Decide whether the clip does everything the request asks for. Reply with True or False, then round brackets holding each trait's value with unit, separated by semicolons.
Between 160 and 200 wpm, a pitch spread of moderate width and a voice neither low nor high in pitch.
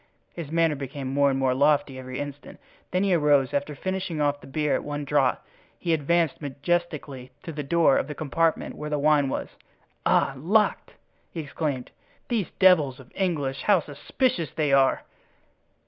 True (175 wpm; 3.3 semitones; 150 Hz)